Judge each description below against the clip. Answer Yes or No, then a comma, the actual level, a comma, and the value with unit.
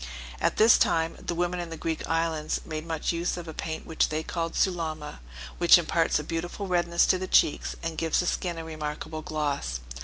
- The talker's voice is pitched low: No, medium, 165 Hz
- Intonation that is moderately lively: No, narrow, 1.7 semitones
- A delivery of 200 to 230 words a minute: Yes, fast, 205 wpm